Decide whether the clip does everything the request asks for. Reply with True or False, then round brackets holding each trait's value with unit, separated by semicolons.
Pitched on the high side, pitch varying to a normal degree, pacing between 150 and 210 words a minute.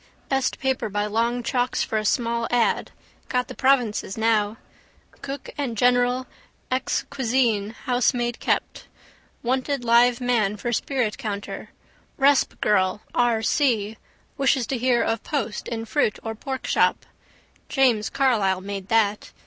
False (240 Hz; 3.1 semitones; 135 wpm)